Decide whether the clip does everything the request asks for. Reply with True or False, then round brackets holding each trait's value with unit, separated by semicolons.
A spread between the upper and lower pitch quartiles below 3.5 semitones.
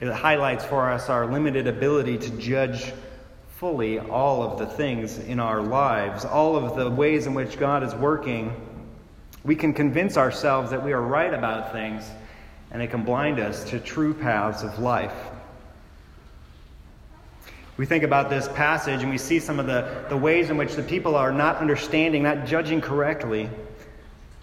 False (4.8 semitones)